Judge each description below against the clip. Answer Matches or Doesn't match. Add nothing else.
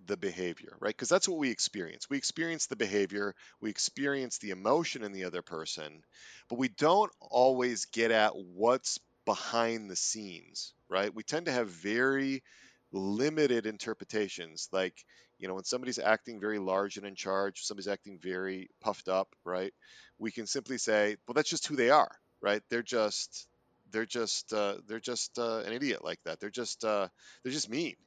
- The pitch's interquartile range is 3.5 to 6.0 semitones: Matches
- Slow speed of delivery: Doesn't match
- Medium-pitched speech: Doesn't match